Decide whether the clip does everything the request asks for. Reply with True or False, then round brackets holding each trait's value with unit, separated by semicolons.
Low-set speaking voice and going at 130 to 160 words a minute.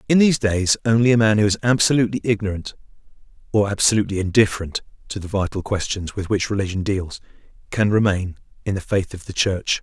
False (100 Hz; 175 wpm)